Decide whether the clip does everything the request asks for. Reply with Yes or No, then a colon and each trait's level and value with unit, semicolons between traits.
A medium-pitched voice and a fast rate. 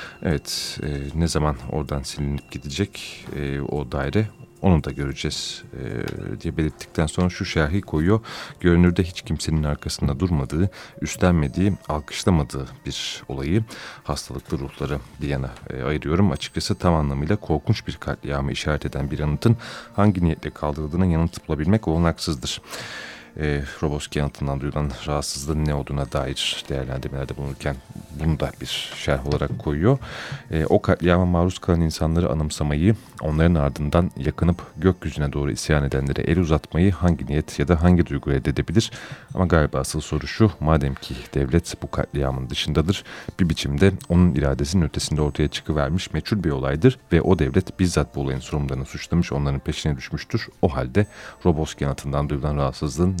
No: very low, 75 Hz; fast, 145 wpm